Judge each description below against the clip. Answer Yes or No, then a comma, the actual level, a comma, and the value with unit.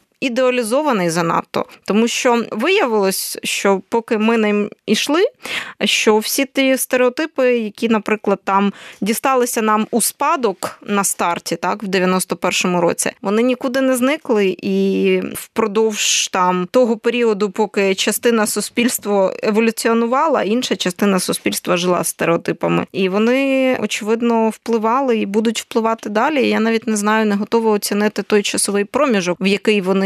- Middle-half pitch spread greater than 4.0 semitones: No, average, 3.3 semitones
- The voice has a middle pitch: No, high, 220 Hz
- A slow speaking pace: No, average, 135 wpm